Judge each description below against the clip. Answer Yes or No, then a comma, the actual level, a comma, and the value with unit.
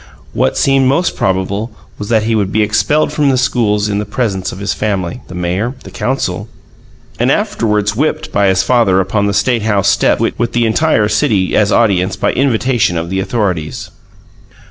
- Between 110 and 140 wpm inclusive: No, average, 185 wpm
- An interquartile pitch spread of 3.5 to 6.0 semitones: Yes, average, 3.9 semitones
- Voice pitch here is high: No, low, 105 Hz